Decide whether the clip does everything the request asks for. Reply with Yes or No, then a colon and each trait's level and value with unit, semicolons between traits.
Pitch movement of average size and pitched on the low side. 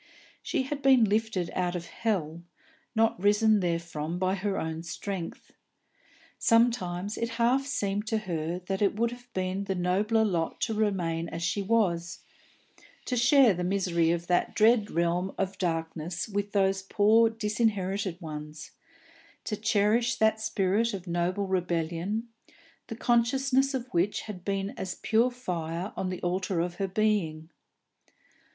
No: average, 4.1 semitones; high, 195 Hz